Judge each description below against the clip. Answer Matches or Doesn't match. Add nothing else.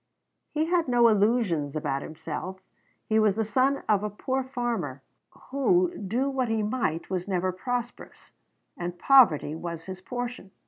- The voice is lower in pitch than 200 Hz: Doesn't match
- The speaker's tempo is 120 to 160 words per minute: Matches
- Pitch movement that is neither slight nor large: Doesn't match